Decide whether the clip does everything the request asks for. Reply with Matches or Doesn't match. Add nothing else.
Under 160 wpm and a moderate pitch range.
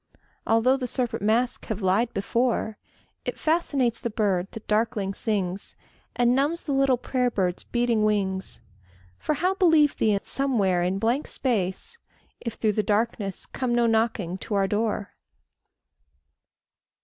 Matches